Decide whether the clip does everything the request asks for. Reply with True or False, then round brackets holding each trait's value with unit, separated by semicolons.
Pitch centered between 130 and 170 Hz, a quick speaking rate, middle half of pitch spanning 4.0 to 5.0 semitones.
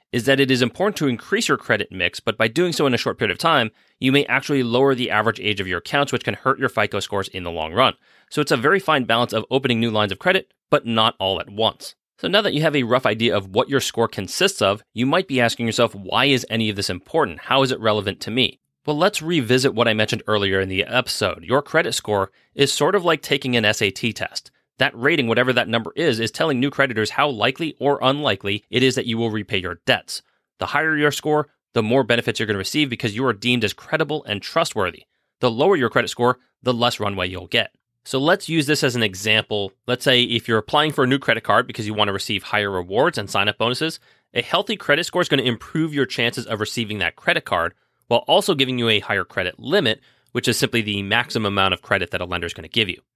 False (120 Hz; 255 wpm; 4.4 semitones)